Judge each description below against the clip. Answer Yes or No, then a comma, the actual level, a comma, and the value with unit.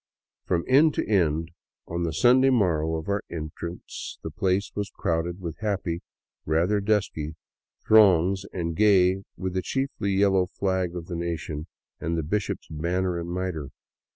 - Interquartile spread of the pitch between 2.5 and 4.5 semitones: Yes, average, 3.2 semitones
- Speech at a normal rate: Yes, average, 155 wpm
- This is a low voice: Yes, very low, 90 Hz